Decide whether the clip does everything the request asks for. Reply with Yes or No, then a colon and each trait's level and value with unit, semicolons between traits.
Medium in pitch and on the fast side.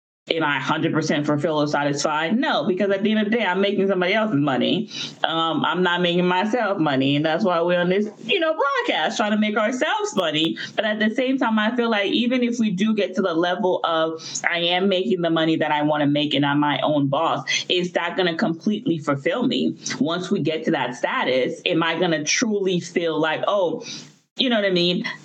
Yes: medium, 180 Hz; fast, 235 wpm